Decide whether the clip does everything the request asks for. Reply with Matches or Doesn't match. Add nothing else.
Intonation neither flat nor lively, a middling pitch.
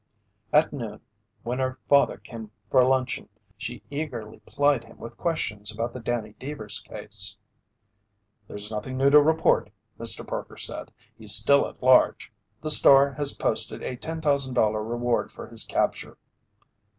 Doesn't match